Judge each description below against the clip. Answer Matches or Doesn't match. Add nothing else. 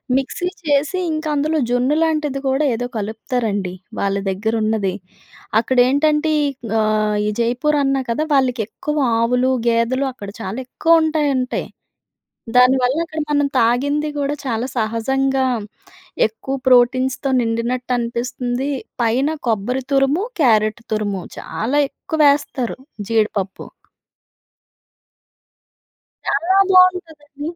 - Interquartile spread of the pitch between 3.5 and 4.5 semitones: Matches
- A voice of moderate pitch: Doesn't match